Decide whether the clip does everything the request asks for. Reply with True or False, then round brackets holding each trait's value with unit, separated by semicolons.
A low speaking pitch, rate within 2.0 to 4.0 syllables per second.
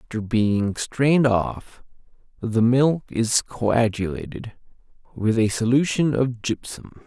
True (120 Hz; 3.8 syllables/s)